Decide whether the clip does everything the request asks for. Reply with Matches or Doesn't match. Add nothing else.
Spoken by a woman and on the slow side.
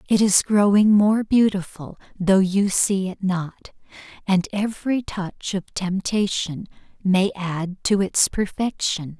Matches